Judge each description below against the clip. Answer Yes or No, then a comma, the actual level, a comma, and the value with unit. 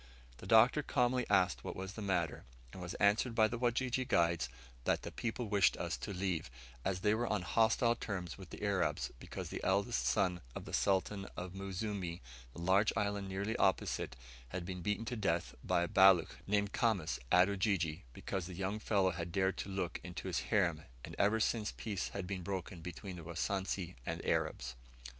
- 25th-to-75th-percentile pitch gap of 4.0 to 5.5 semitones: No, average, 2.9 semitones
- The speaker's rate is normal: Yes, average, 190 wpm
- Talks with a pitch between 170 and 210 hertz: No, very low, 95 Hz